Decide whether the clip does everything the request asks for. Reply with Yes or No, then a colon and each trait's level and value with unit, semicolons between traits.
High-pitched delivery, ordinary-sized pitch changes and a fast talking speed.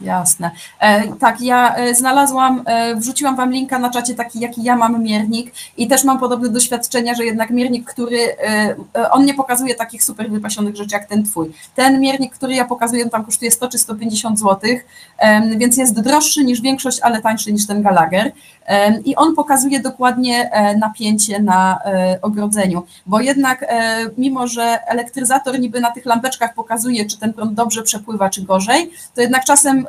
Yes: high, 235 Hz; average, 3.0 semitones; fast, 165 wpm